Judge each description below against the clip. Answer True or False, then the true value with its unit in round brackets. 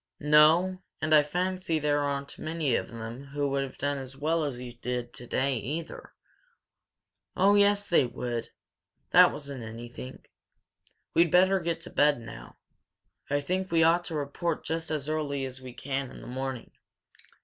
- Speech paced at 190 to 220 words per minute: False (165 wpm)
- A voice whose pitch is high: False (145 Hz)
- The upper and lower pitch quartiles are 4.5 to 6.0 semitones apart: False (4.1 semitones)